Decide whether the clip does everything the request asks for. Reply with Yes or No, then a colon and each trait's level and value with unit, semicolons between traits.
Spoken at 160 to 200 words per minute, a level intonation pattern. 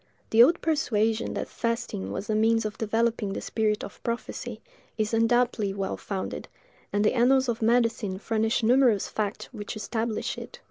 Yes: average, 165 wpm; narrow, 2.0 semitones